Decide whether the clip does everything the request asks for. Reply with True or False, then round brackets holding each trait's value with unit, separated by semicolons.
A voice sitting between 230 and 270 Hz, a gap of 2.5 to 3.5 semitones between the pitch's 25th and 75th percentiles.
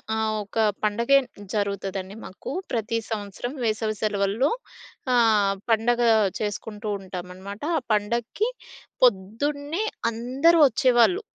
False (220 Hz; 3.2 semitones)